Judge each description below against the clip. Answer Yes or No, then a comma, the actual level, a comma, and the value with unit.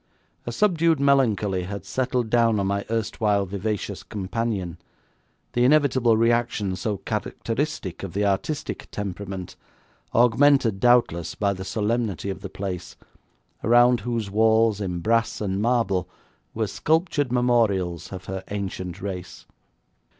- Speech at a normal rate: No, slow, 125 wpm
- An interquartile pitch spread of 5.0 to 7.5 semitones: No, average, 3.7 semitones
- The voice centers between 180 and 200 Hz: No, low, 105 Hz